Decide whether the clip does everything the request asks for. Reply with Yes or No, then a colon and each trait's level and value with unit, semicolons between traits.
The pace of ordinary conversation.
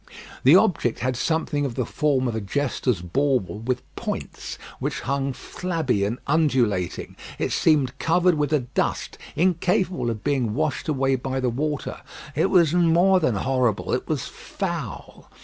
Yes: average, 155 wpm